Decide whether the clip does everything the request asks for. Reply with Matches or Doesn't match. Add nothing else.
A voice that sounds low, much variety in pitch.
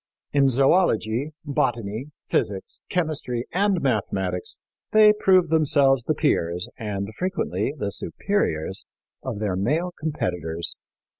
Matches